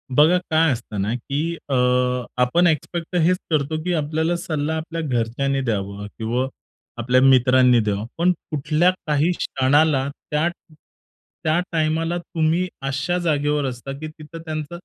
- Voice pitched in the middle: Yes, medium, 150 Hz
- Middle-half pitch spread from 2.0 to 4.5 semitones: Yes, average, 3.9 semitones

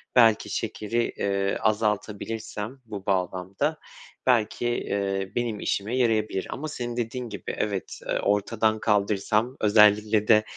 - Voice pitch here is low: Yes, low, 110 Hz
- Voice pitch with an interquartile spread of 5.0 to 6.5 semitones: No, narrow, 2.4 semitones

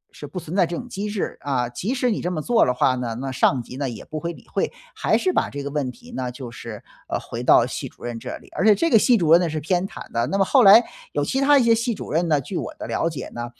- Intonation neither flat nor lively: No, wide, 8.1 semitones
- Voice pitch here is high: No, medium, 165 Hz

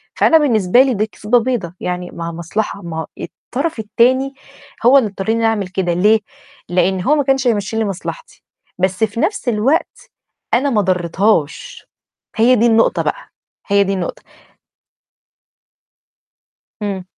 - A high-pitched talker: Yes, high, 215 Hz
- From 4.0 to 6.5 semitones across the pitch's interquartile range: Yes, average, 5.0 semitones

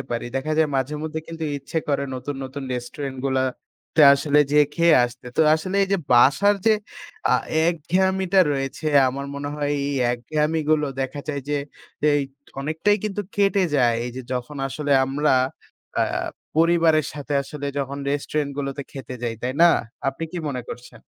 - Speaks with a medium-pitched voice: Yes, medium, 145 Hz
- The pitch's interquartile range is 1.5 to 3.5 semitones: Yes, average, 3.0 semitones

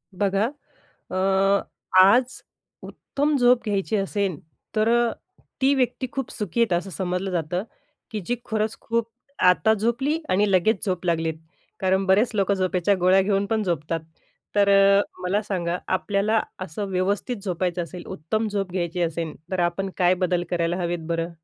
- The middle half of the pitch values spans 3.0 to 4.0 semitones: Yes, average, 3.4 semitones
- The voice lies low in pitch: No, high, 190 Hz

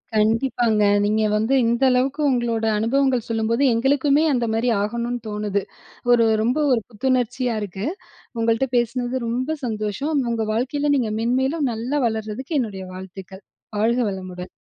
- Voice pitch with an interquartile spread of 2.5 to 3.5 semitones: Yes, average, 3.2 semitones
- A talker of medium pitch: No, high, 235 Hz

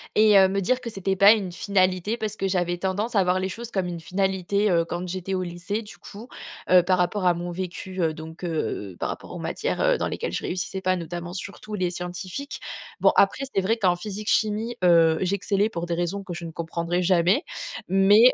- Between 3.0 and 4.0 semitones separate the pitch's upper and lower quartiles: No, narrow, 2.5 semitones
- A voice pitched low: No, medium, 185 Hz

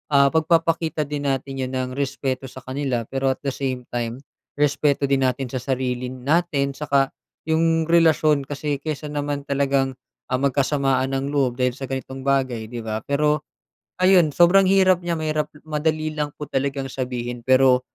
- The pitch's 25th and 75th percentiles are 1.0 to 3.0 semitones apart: Yes, narrow, 2.6 semitones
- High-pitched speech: No, medium, 140 Hz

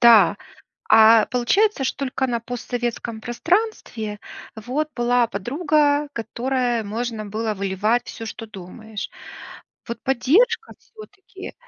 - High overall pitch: Yes, high, 240 Hz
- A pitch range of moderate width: Yes, average, 4.2 semitones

